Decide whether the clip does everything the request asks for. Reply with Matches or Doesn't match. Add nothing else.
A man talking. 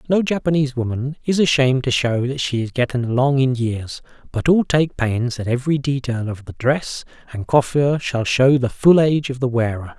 Matches